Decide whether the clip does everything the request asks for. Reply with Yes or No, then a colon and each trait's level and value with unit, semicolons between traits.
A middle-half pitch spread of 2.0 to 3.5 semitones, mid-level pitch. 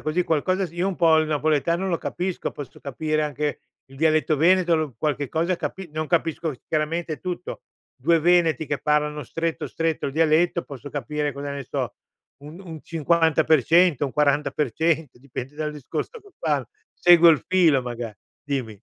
Yes: narrow, 2.6 semitones; medium, 155 Hz